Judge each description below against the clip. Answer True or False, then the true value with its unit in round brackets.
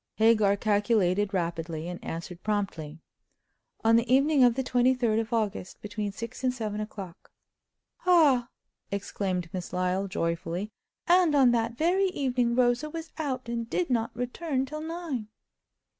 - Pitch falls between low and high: False (230 Hz)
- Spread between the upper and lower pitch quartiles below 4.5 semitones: False (4.8 semitones)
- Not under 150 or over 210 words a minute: False (140 wpm)